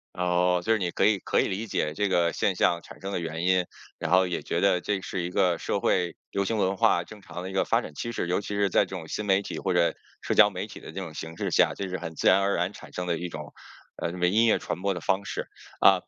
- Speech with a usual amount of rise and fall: No, narrow, 2.2 semitones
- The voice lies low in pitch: Yes, very low, 90 Hz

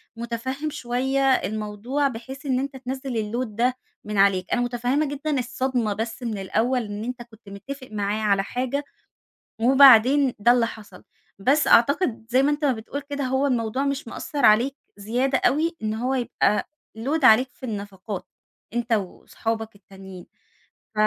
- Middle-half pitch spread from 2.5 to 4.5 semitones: Yes, average, 3.7 semitones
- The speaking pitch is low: No, high, 245 Hz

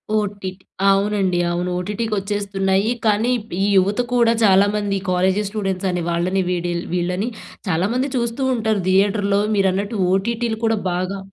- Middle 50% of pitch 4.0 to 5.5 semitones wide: No, narrow, 2.4 semitones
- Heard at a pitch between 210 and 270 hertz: No, high, 200 Hz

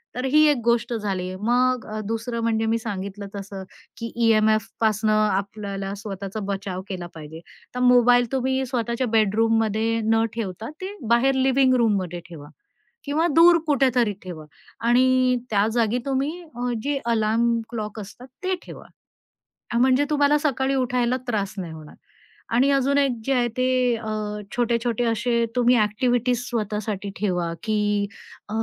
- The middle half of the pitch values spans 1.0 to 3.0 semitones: No, average, 3.4 semitones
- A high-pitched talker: Yes, high, 230 Hz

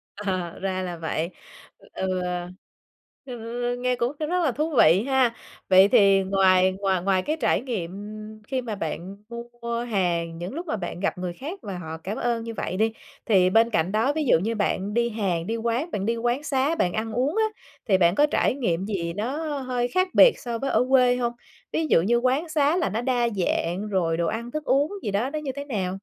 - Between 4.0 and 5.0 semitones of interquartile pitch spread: No, wide, 5.5 semitones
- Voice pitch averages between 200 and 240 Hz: Yes, high, 225 Hz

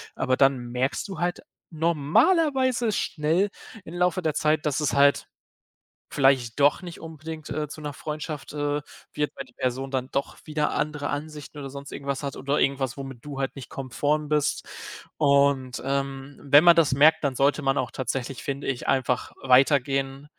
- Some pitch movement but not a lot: No, narrow, 2.3 semitones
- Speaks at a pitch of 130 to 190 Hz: Yes, medium, 140 Hz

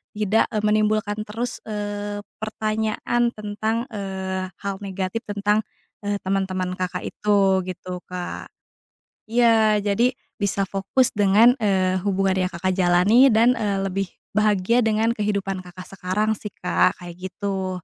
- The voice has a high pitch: Yes, high, 205 Hz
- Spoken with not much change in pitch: Yes, narrow, 2.3 semitones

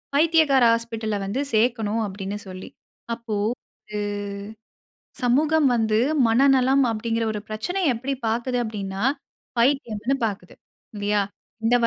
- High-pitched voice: Yes, high, 230 Hz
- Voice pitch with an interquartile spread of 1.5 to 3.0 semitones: No, average, 3.7 semitones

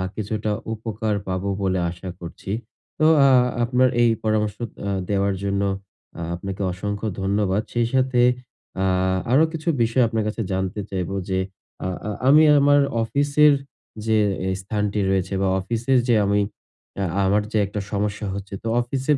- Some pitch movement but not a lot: Yes, average, 3.5 semitones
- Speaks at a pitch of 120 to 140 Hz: No, low, 105 Hz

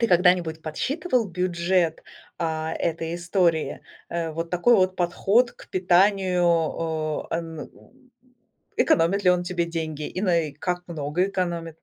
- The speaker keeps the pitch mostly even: Yes, narrow, 2.0 semitones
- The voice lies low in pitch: No, medium, 175 Hz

